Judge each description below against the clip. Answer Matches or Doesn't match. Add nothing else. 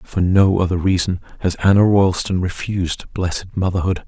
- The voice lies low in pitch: Matches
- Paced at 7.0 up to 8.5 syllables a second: Doesn't match